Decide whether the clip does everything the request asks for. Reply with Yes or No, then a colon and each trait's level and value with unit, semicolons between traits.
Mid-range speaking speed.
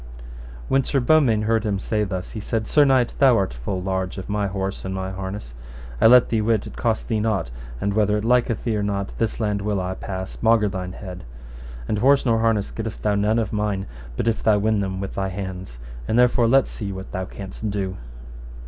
No: fast, 220 wpm